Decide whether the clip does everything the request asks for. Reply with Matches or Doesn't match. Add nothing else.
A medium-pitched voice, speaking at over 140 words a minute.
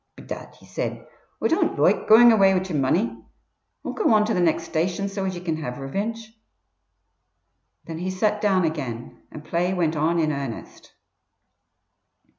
Matches